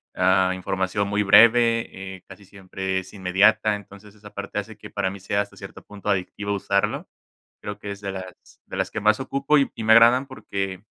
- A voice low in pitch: Yes, low, 100 Hz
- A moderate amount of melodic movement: No, narrow, 2.3 semitones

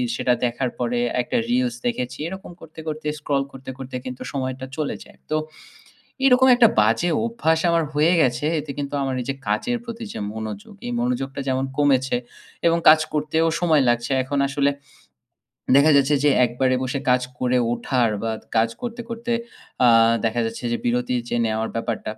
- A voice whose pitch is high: No, low, 135 Hz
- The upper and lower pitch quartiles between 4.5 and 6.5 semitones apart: Yes, average, 4.8 semitones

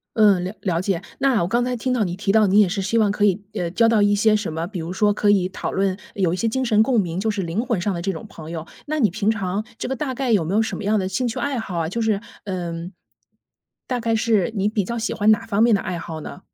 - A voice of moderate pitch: No, high, 205 Hz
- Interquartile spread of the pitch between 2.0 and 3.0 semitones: No, average, 3.4 semitones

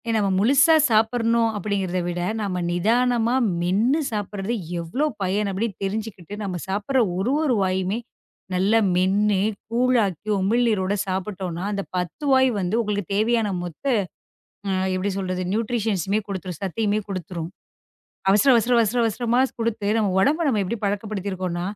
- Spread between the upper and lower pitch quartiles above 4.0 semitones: No, average, 3.5 semitones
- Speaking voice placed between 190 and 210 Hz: Yes, high, 205 Hz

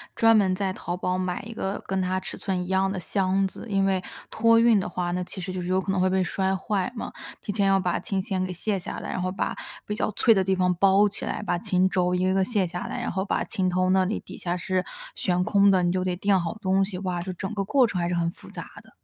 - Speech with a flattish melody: Yes, narrow, 1.4 semitones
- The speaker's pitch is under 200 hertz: Yes, high, 190 Hz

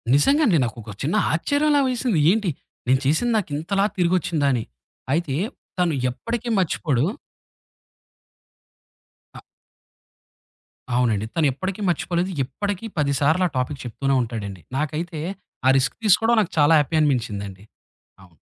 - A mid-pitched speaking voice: Yes, medium, 155 Hz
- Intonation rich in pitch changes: Yes, wide, 6.5 semitones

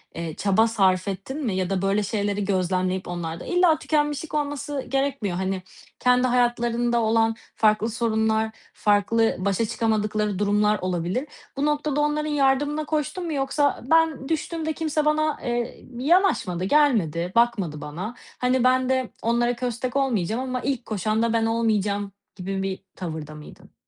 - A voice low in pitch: No, high, 230 Hz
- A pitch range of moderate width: No, wide, 5.9 semitones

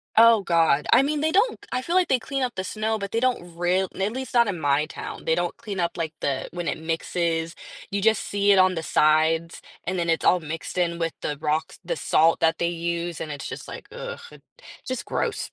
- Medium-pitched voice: Yes, medium, 175 Hz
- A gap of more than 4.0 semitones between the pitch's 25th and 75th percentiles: Yes, wide, 5.6 semitones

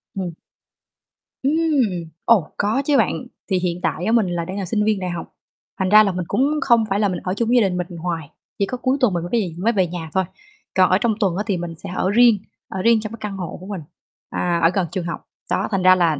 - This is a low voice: No, high, 190 Hz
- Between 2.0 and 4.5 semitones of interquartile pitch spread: Yes, average, 3.9 semitones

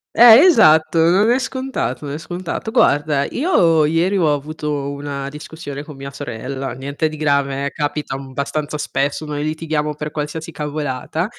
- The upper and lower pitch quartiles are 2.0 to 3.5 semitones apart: Yes, narrow, 2.5 semitones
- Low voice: No, medium, 150 Hz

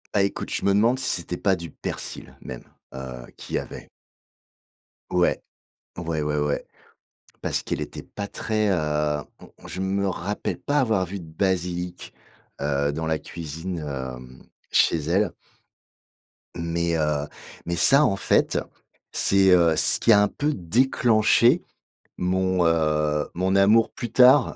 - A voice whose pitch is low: Yes, very low, 90 Hz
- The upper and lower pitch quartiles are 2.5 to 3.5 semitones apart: No, average, 4.8 semitones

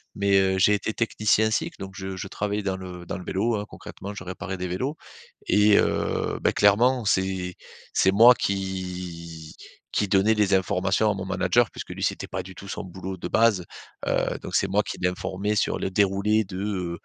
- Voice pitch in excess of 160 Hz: No, very low, 95 Hz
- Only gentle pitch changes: Yes, narrow, 2.0 semitones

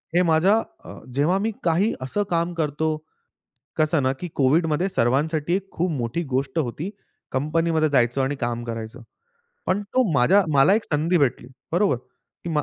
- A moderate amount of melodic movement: Yes, average, 4.6 semitones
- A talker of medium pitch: Yes, medium, 155 Hz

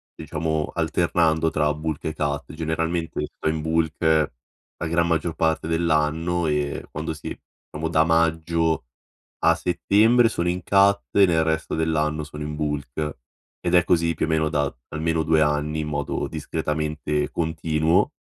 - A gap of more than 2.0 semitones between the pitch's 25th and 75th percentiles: No, narrow, 1.4 semitones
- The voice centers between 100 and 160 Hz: No, very low, 80 Hz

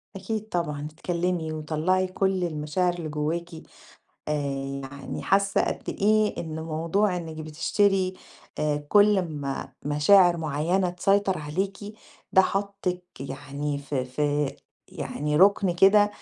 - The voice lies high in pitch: No, medium, 170 Hz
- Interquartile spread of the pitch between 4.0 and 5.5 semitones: Yes, average, 4.4 semitones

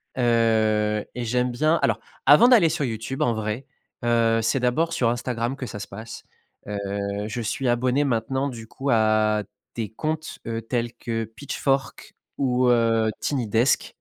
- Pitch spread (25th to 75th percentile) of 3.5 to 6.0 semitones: No, average, 3.0 semitones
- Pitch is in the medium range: No, low, 120 Hz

